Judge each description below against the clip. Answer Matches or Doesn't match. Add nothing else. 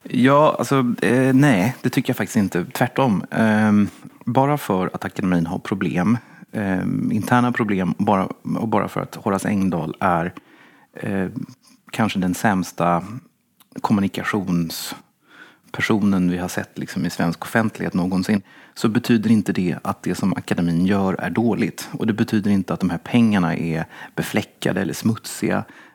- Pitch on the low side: Matches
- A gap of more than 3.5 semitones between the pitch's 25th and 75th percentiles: Matches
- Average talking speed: Matches